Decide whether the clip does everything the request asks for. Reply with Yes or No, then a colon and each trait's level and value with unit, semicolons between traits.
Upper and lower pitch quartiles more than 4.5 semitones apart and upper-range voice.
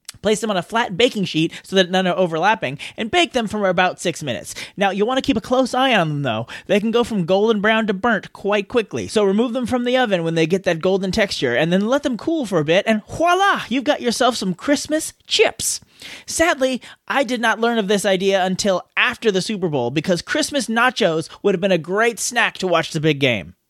Yes: average, 5.2 semitones; high, 210 Hz